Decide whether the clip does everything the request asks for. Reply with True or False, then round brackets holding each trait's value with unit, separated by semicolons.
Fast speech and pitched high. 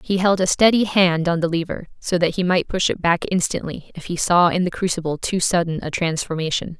False (230 wpm; 175 Hz)